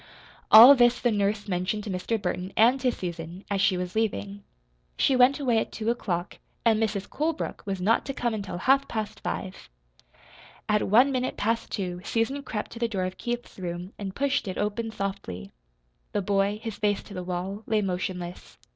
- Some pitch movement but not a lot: Yes, average, 3.8 semitones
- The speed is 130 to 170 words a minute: No, average, 190 wpm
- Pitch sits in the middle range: No, high, 205 Hz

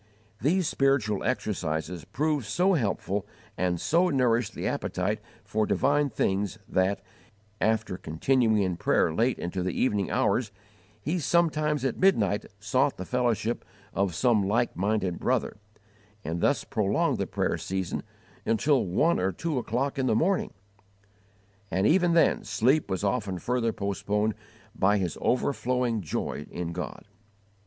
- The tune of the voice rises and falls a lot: Yes, wide, 5.9 semitones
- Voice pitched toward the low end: Yes, low, 110 Hz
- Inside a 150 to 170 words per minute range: No, average, 140 wpm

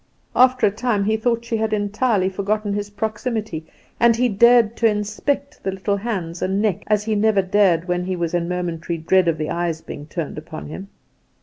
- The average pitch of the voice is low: No, high, 205 Hz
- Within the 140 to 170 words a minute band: No, average, 200 wpm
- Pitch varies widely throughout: No, average, 3.7 semitones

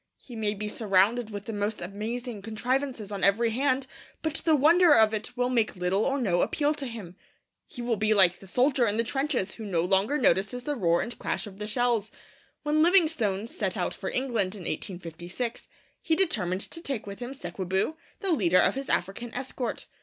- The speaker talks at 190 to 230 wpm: Yes, average, 200 wpm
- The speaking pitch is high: Yes, high, 225 Hz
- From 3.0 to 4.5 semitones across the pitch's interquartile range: No, average, 5.1 semitones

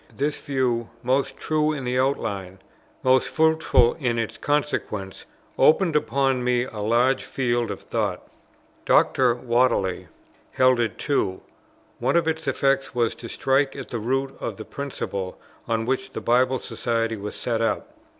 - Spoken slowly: No, average, 150 wpm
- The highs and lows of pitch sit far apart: No, average, 2.9 semitones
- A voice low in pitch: Yes, low, 125 Hz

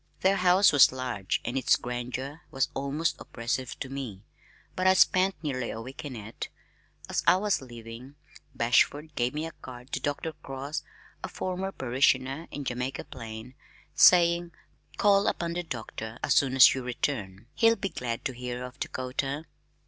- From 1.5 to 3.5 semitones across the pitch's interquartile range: No, average, 4.8 semitones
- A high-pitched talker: No, low, 135 Hz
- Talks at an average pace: Yes, average, 165 wpm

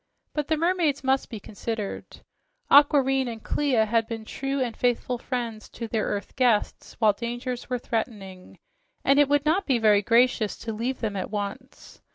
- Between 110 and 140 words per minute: No, average, 175 wpm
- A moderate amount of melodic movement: Yes, average, 3.6 semitones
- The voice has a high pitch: Yes, high, 240 Hz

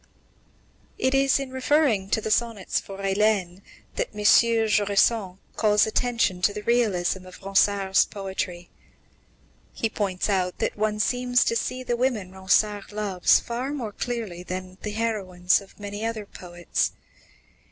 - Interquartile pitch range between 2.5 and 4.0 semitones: Yes, average, 3.3 semitones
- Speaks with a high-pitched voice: Yes, high, 210 Hz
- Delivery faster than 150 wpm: No, average, 140 wpm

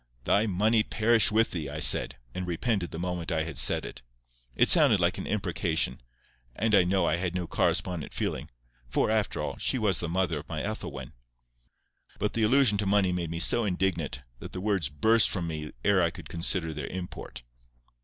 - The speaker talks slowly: No, average, 195 wpm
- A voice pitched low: Yes, very low, 90 Hz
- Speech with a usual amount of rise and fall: Yes, average, 4.1 semitones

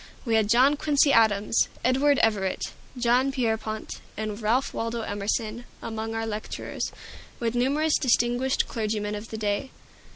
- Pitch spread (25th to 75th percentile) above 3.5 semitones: No, average, 3.0 semitones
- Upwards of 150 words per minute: No, slow, 135 wpm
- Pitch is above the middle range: Yes, high, 225 Hz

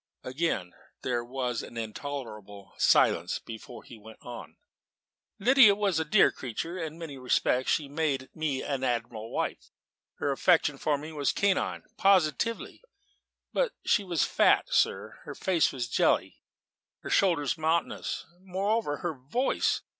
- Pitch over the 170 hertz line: No, medium, 145 Hz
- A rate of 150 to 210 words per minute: No, average, 140 wpm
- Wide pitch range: Yes, wide, 6.3 semitones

